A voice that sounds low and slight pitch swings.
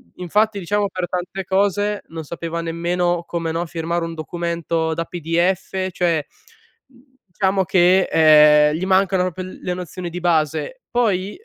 No: medium, 175 Hz; narrow, 2.3 semitones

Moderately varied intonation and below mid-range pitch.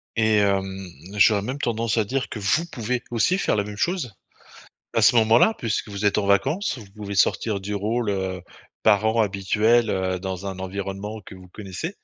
Yes: average, 3.0 semitones; low, 105 Hz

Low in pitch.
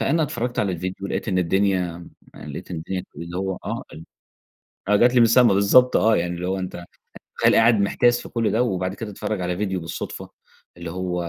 Yes: very low, 95 Hz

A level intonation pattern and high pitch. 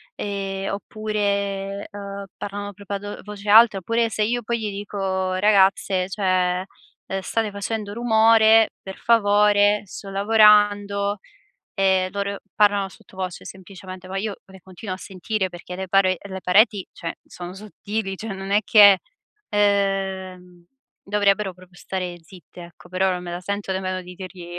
Yes: narrow, 1.7 semitones; high, 200 Hz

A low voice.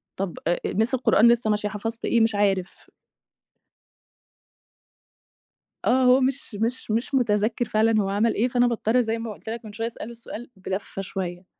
No: high, 225 Hz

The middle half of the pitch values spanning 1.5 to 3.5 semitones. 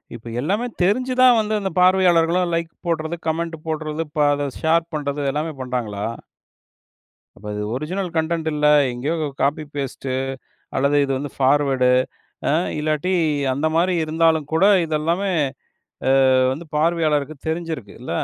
Yes: average, 3.0 semitones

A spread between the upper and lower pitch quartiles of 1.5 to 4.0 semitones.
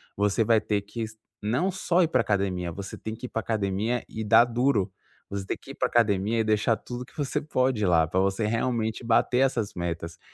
Yes: average, 3.4 semitones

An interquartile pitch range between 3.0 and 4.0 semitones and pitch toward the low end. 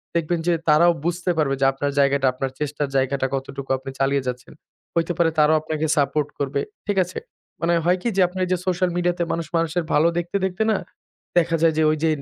No: average, 3.7 semitones; medium, 160 Hz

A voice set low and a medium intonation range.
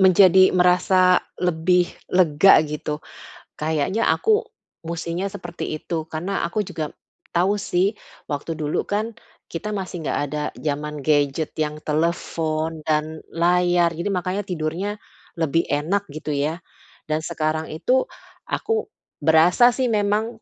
No: medium, 170 Hz; average, 3.5 semitones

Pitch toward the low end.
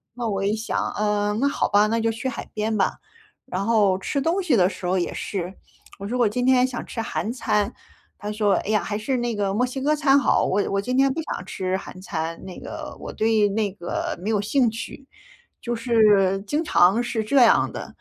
No: high, 215 Hz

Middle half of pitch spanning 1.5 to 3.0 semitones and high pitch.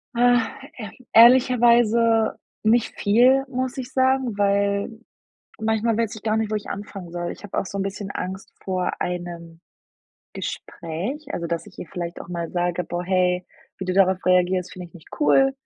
No: average, 4.7 semitones; high, 200 Hz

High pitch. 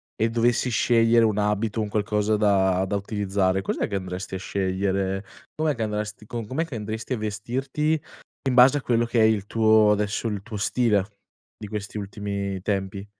No: low, 105 Hz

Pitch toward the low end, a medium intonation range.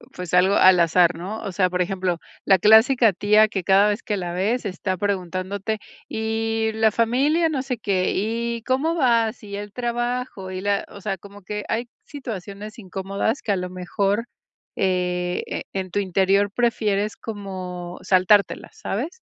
No: high, 205 Hz; average, 3.2 semitones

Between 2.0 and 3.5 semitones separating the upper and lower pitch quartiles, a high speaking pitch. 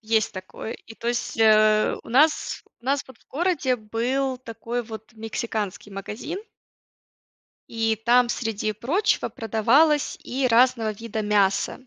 Yes: average, 2.9 semitones; high, 230 Hz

